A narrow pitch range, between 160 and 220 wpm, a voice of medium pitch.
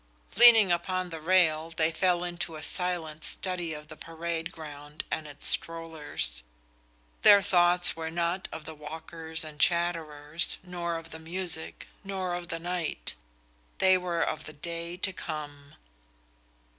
No: narrow, 2.1 semitones; average, 145 wpm; medium, 165 Hz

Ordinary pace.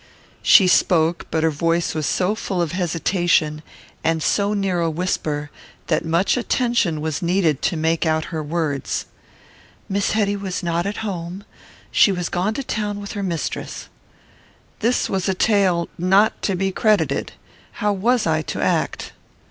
Yes: average, 160 wpm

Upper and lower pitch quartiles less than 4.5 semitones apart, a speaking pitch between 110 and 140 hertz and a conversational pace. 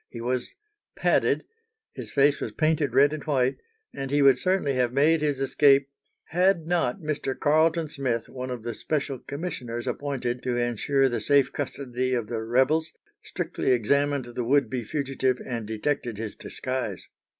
Yes: average, 3.1 semitones; low, 135 Hz; average, 160 wpm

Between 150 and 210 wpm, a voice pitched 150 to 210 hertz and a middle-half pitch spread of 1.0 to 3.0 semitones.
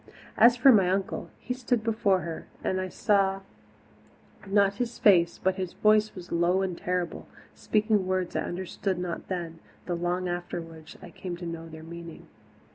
Yes: average, 170 wpm; medium, 185 Hz; narrow, 2.6 semitones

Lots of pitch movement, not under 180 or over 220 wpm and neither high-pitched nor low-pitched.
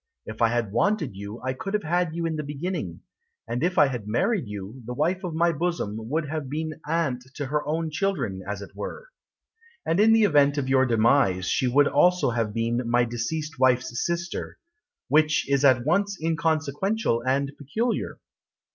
Yes: wide, 5.7 semitones; average, 185 wpm; medium, 145 Hz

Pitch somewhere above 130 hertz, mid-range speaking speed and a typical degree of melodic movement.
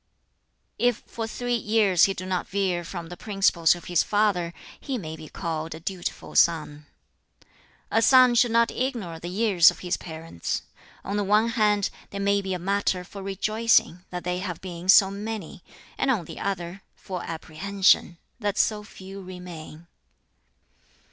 Yes: high, 190 Hz; average, 165 wpm; average, 3.4 semitones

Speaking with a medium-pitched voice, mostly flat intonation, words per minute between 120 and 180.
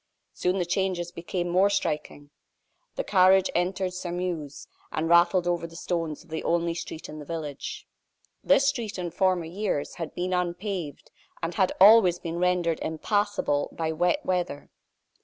Yes: medium, 175 Hz; narrow, 2.2 semitones; average, 155 wpm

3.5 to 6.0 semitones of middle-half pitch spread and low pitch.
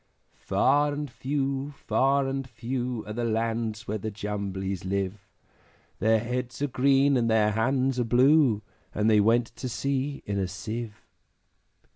Yes: average, 4.0 semitones; low, 120 Hz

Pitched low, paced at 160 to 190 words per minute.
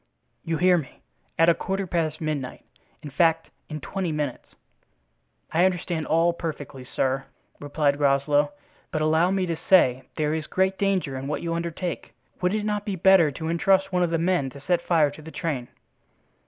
No: medium, 165 Hz; average, 175 wpm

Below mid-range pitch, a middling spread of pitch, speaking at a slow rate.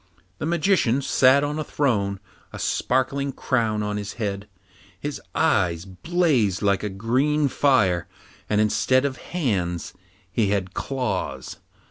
No: low, 120 Hz; wide, 6.0 semitones; slow, 130 wpm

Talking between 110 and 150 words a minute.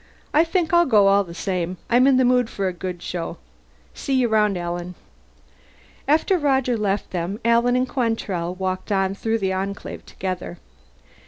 No: average, 170 wpm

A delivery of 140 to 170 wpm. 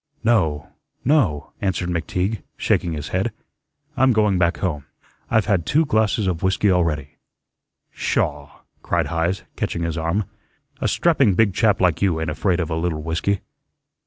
Yes: average, 155 wpm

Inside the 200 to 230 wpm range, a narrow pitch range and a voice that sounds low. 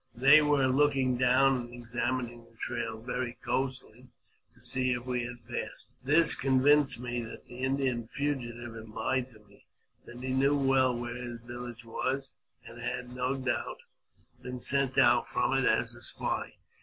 No: average, 170 wpm; narrow, 1.9 semitones; low, 125 Hz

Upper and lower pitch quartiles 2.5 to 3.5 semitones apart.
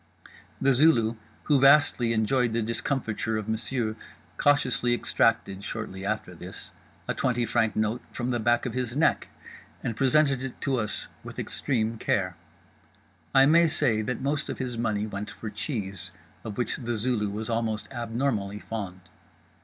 Yes: average, 3.1 semitones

